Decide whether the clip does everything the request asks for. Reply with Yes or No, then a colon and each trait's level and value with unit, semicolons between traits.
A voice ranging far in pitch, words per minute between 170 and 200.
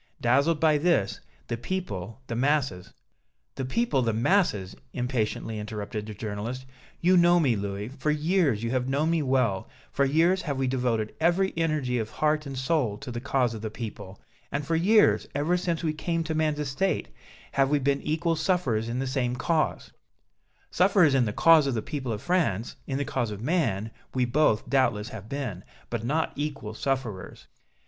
Yes: wide, 5.7 semitones; average, 185 wpm